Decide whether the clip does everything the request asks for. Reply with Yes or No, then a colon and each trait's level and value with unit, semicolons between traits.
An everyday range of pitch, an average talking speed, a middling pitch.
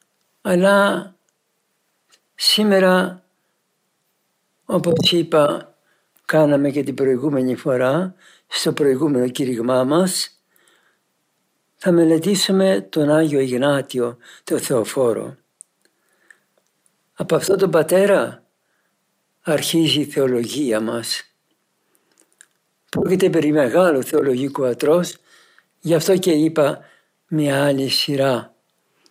No: average, 5.0 semitones; slow, 80 wpm; medium, 155 Hz